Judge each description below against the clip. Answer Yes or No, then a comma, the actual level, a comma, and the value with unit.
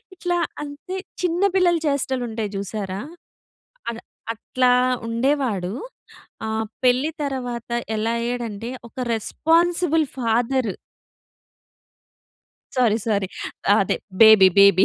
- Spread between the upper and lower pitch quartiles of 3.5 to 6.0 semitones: Yes, average, 4.7 semitones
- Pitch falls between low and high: No, high, 240 Hz